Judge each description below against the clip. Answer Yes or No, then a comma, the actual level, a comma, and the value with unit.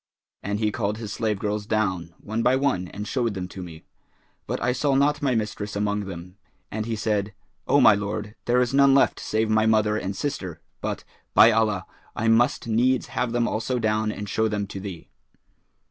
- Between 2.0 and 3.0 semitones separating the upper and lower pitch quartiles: Yes, narrow, 2.4 semitones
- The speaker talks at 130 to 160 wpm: No, average, 200 wpm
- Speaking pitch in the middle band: No, low, 110 Hz